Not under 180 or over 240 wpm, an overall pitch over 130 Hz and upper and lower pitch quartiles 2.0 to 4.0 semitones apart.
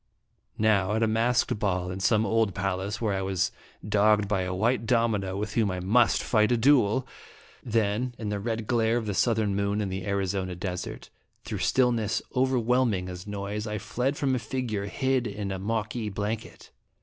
No: average, 185 wpm; low, 105 Hz; average, 2.8 semitones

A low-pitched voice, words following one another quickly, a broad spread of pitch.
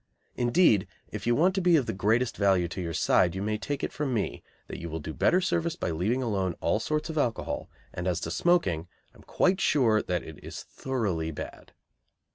Yes: low, 110 Hz; fast, 215 wpm; wide, 8.6 semitones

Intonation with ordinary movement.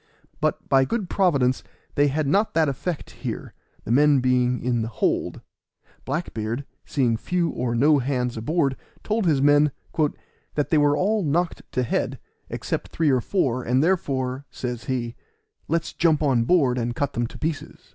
Yes: average, 4.1 semitones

